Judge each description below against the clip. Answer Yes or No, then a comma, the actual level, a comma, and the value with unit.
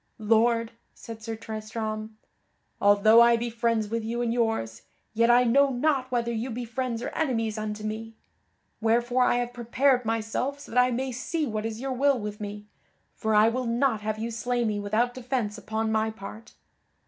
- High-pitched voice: Yes, high, 230 Hz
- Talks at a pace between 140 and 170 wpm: No, average, 185 wpm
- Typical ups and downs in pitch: No, narrow, 2.1 semitones